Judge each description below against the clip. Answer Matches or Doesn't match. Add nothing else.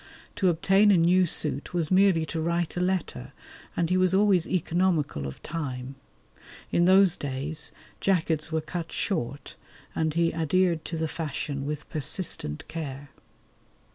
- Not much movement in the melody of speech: Doesn't match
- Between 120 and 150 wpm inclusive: Matches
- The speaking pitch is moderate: Matches